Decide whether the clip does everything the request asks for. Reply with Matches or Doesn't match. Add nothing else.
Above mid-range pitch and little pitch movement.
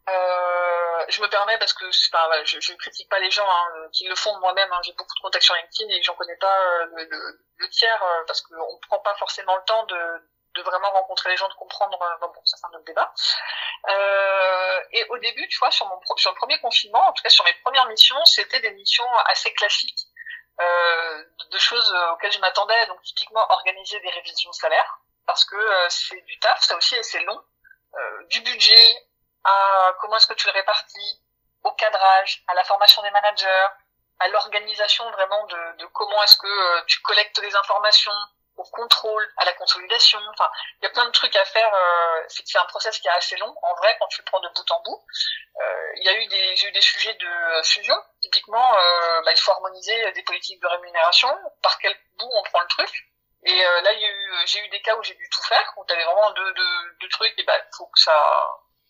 Doesn't match